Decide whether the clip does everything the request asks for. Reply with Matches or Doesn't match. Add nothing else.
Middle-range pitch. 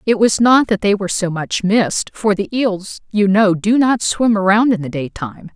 Doesn't match